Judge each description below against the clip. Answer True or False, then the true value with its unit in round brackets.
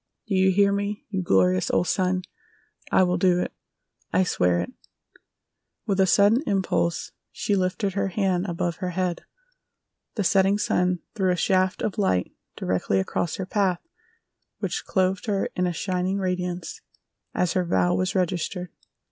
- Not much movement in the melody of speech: True (1.8 semitones)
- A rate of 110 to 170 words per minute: True (155 wpm)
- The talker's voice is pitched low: False (185 Hz)